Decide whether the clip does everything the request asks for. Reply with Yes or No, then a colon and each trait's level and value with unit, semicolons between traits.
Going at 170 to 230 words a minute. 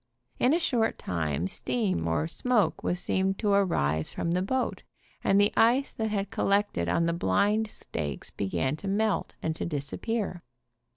Yes: average, 185 wpm